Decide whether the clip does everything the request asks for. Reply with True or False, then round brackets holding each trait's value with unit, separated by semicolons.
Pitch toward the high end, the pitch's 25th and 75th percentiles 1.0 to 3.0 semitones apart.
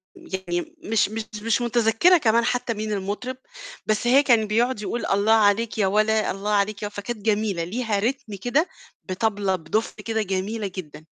True (215 Hz; 2.6 semitones)